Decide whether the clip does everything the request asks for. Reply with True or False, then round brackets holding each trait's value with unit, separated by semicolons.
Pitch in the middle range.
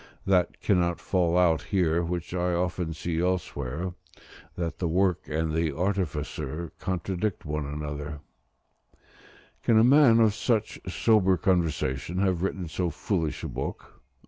False (90 Hz)